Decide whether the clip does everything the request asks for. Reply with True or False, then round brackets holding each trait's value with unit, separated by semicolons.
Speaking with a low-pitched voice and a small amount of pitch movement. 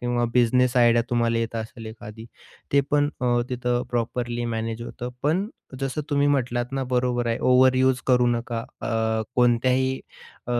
True (120 Hz; 1.6 semitones)